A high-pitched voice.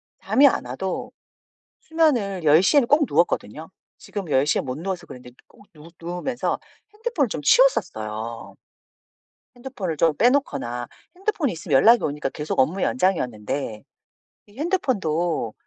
No: medium, 175 Hz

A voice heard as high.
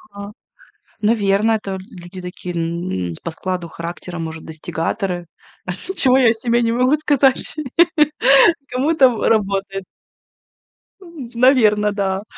Yes: high, 200 Hz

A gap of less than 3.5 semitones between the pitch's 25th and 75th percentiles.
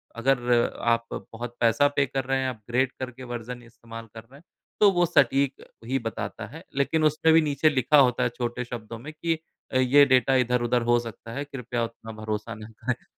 Yes: average, 2.8 semitones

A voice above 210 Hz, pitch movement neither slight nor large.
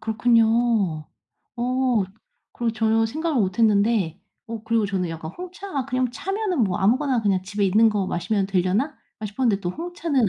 Yes: high, 225 Hz; average, 4.4 semitones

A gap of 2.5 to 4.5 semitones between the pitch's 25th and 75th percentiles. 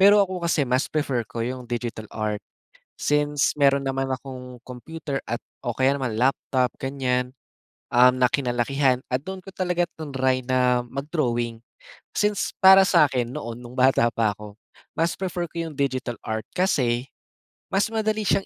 Yes: average, 4.0 semitones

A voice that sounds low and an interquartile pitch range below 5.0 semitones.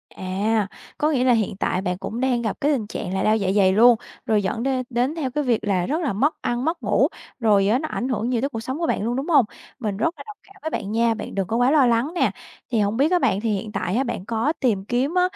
No: high, 235 Hz; average, 4.5 semitones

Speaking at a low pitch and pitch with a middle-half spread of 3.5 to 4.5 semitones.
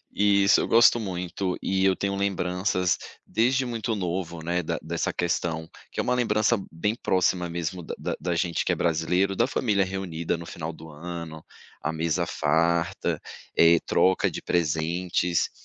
No: very low, 90 Hz; average, 2.9 semitones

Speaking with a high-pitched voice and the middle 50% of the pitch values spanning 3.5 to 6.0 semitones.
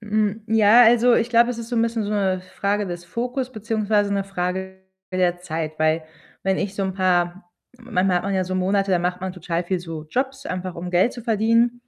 Yes: high, 195 Hz; average, 4.0 semitones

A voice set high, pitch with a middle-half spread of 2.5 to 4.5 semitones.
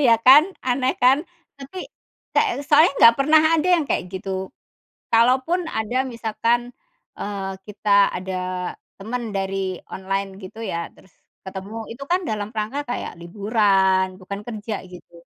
No: high, 215 Hz; average, 4.9 semitones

